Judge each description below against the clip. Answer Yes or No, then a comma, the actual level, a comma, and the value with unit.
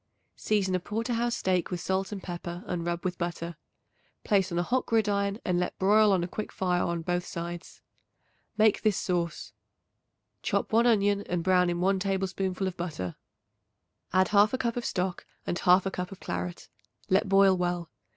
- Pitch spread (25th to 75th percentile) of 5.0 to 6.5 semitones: No, narrow, 2.4 semitones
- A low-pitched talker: No, medium, 185 Hz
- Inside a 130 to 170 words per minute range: No, average, 180 wpm